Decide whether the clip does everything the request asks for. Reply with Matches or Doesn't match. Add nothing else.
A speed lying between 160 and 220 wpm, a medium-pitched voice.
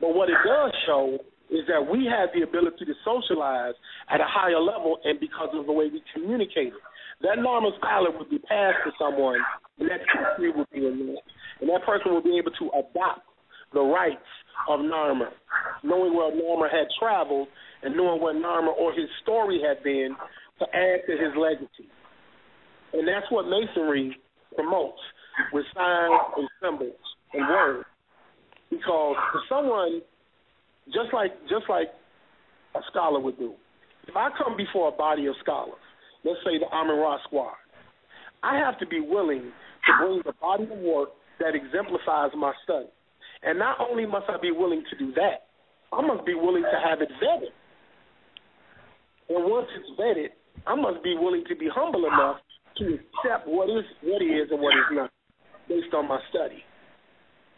Matches